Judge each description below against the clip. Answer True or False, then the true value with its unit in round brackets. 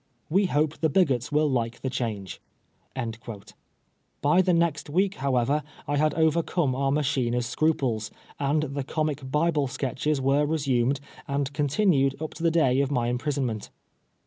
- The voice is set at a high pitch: False (140 Hz)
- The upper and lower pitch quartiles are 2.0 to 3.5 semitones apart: True (2.9 semitones)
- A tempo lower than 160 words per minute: True (145 wpm)